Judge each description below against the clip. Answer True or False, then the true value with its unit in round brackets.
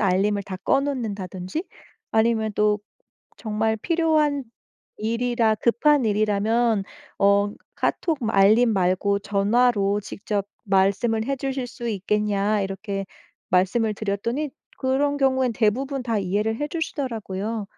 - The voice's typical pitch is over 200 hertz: True (220 Hz)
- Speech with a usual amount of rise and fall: True (3.7 semitones)